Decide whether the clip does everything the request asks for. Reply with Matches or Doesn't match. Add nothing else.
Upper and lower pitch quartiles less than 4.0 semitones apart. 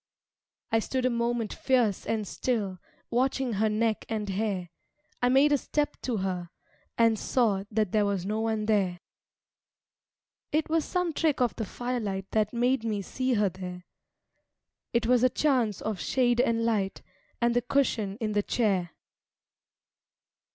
Matches